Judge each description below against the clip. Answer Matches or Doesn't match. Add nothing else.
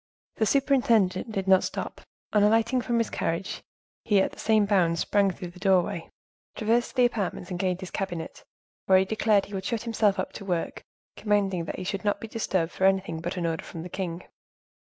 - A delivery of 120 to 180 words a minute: Doesn't match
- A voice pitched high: Matches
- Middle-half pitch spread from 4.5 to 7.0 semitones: Doesn't match